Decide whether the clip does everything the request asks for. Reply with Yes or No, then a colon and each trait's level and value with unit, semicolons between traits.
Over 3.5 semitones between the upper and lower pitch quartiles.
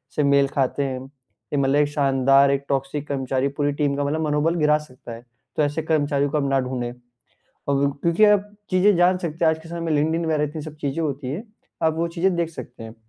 No: average, 2.8 semitones